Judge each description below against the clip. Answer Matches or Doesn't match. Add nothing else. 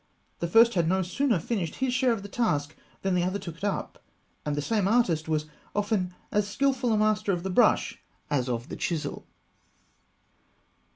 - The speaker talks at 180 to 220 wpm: Matches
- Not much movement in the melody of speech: Doesn't match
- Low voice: Doesn't match